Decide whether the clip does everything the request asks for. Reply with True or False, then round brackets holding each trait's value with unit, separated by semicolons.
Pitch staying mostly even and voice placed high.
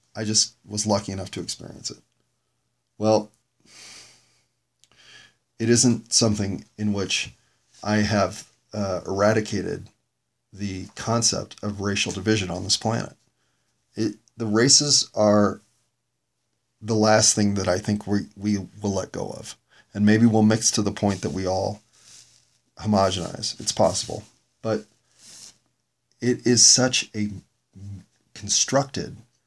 False (2.3 semitones; 105 Hz)